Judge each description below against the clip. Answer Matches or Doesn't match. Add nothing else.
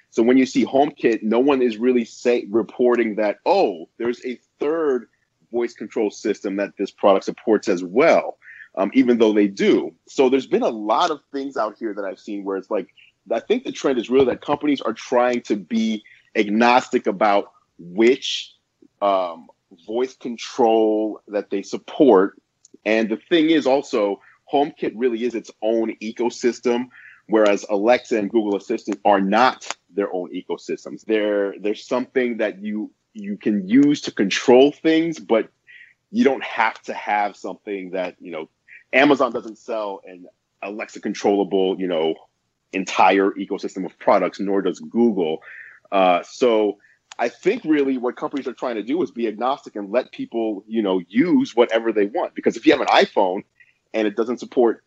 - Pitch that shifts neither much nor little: Matches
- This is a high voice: Doesn't match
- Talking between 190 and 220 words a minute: Doesn't match